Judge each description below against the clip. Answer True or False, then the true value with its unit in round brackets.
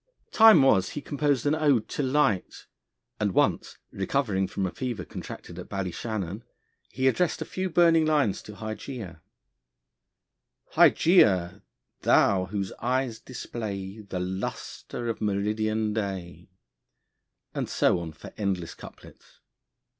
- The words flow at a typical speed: False (125 wpm)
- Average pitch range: False (5.7 semitones)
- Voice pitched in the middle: False (110 Hz)